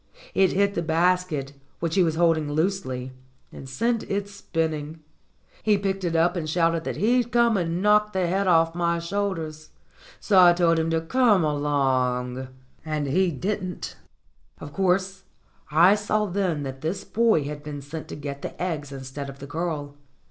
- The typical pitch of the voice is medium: Yes, medium, 165 Hz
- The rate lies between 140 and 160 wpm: No, average, 175 wpm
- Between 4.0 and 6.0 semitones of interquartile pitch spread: Yes, average, 4.5 semitones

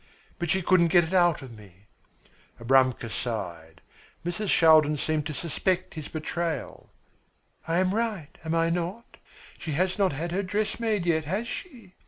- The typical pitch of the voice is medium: Yes, medium, 170 Hz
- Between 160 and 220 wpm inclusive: Yes, average, 165 wpm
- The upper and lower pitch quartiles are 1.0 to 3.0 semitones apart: No, average, 4.2 semitones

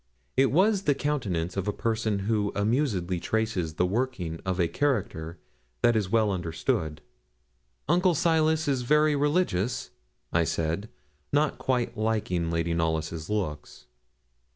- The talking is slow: Yes, slow, 130 wpm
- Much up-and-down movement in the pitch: Yes, wide, 8.1 semitones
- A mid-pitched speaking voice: No, low, 105 Hz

